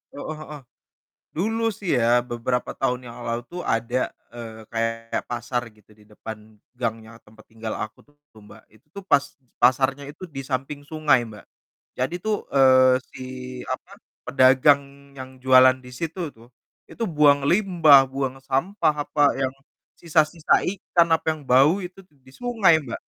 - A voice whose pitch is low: Yes, low, 130 Hz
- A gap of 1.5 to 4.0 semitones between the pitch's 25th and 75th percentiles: No, average, 4.4 semitones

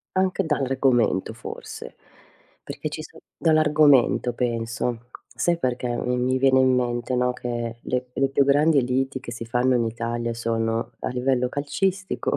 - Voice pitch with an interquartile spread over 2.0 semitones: Yes, narrow, 2.5 semitones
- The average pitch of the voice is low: Yes, low, 125 Hz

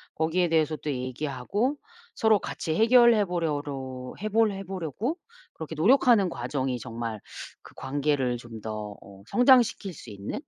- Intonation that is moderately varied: No, wide, 9.0 semitones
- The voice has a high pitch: No, medium, 160 Hz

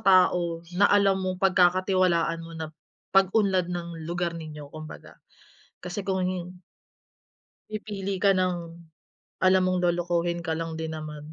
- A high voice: No, medium, 180 Hz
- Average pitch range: No, narrow, 2.1 semitones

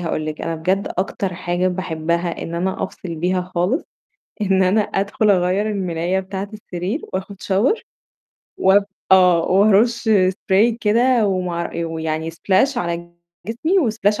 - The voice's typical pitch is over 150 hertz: Yes, medium, 185 Hz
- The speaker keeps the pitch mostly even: No, average, 3.1 semitones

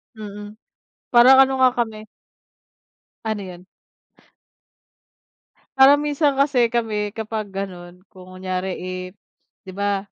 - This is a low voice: No, high, 210 Hz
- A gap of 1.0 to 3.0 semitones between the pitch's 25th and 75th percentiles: No, average, 4.5 semitones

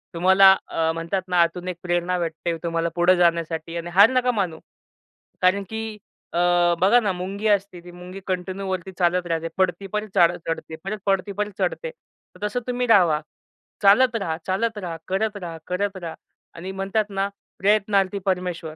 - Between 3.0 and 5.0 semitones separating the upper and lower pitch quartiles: No, narrow, 2.6 semitones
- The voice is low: No, medium, 185 Hz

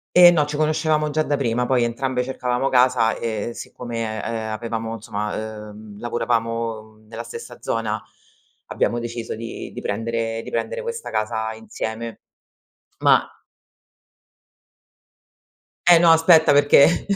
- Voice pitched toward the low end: Yes, low, 115 Hz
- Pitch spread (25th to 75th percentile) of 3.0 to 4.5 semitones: Yes, average, 3.5 semitones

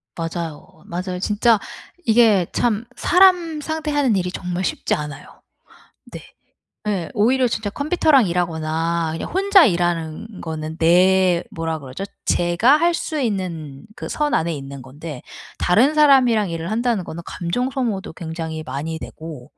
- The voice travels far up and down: Yes, wide, 6.8 semitones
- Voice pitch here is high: No, medium, 180 Hz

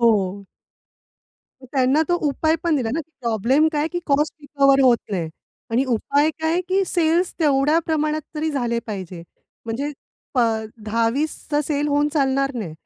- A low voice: No, very high, 280 Hz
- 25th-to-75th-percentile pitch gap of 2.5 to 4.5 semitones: No, average, 4.9 semitones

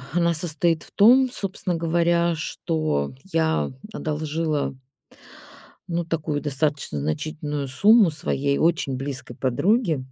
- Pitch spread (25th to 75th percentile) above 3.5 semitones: No, average, 2.9 semitones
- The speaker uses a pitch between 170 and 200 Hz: No, medium, 160 Hz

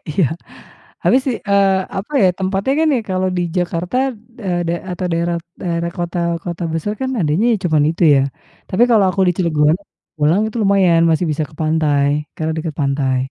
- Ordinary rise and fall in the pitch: Yes, average, 3.5 semitones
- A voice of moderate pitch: Yes, medium, 175 Hz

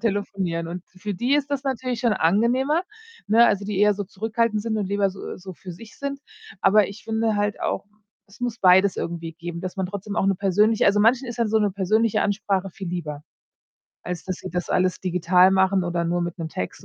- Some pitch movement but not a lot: Yes, average, 3.5 semitones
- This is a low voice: No, high, 200 Hz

